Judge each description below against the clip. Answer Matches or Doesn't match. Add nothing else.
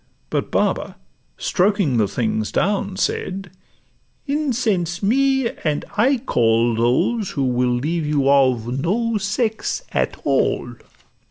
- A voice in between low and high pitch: Matches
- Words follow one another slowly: Matches